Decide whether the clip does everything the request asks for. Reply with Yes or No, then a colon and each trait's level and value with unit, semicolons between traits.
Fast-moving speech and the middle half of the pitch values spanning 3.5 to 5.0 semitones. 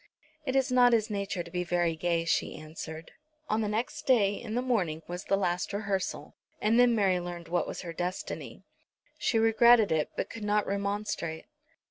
No: average, 185 wpm; average, 4.2 semitones